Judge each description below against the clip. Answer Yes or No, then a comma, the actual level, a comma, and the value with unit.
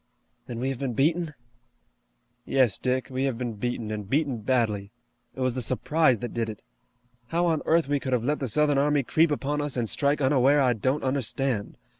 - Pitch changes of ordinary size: Yes, average, 3.3 semitones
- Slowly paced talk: No, average, 200 wpm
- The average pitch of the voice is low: Yes, low, 130 Hz